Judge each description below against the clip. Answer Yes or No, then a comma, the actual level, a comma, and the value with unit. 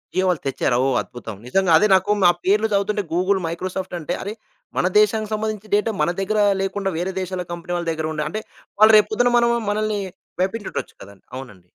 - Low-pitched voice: No, high, 190 Hz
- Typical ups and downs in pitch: Yes, average, 3.8 semitones